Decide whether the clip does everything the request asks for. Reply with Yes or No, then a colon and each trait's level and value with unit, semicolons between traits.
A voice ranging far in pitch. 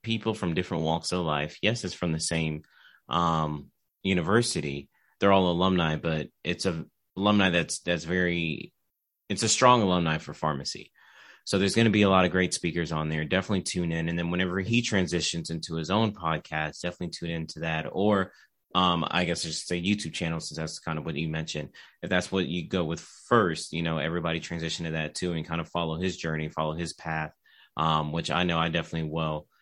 No: narrow, 2.5 semitones